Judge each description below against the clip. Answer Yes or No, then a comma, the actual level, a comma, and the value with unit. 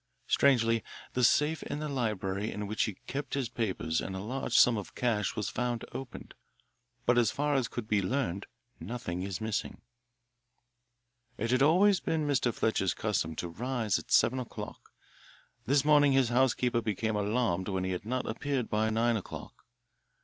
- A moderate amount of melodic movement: Yes, average, 4.2 semitones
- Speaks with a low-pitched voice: Yes, low, 115 Hz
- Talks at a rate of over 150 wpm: Yes, average, 170 wpm